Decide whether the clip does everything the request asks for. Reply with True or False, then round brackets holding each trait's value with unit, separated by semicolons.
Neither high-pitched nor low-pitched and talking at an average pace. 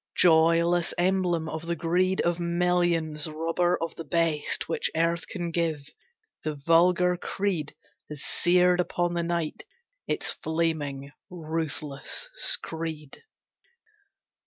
False (165 Hz; 110 wpm)